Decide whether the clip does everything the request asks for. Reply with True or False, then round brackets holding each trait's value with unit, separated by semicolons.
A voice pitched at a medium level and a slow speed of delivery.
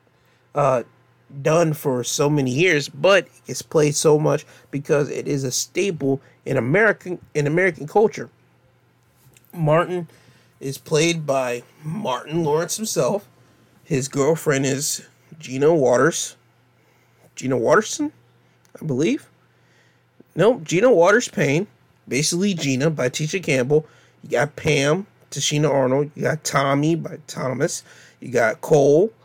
True (150 Hz; 120 wpm)